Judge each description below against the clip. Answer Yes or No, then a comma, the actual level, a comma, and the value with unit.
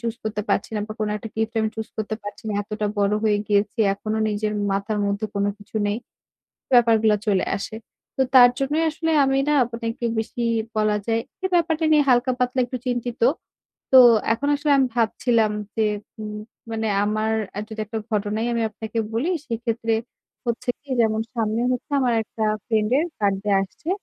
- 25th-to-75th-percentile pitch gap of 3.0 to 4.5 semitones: No, narrow, 2.4 semitones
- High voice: Yes, high, 220 Hz